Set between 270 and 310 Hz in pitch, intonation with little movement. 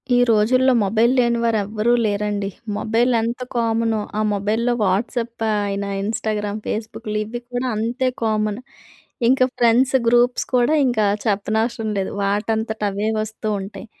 No: high, 220 Hz; narrow, 2.1 semitones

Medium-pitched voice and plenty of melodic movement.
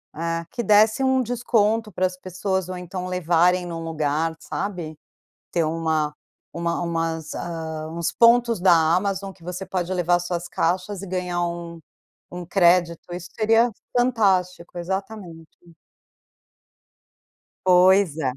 No: medium, 180 Hz; average, 2.7 semitones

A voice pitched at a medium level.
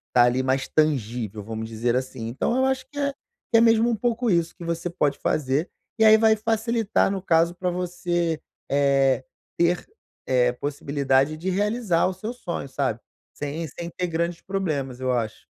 Yes: medium, 165 Hz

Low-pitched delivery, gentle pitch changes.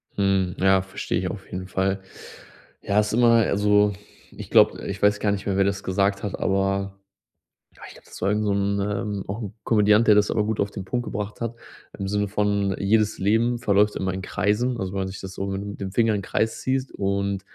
Yes: low, 100 Hz; narrow, 1.3 semitones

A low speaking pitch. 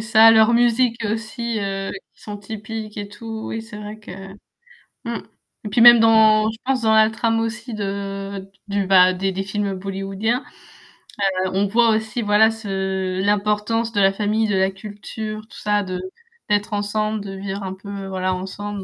No: high, 210 Hz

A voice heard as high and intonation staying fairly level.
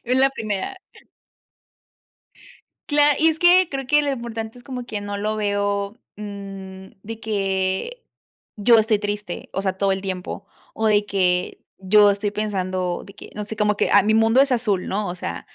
No: high, 210 Hz; average, 3.1 semitones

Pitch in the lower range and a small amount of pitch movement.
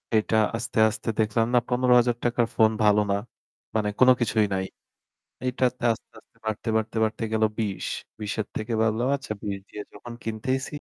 Yes: low, 110 Hz; narrow, 2.3 semitones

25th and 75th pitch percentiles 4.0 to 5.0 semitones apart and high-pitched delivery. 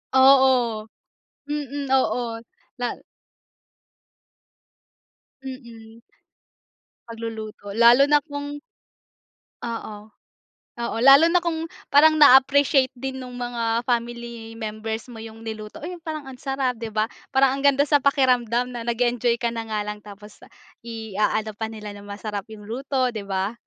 No: average, 3.4 semitones; high, 240 Hz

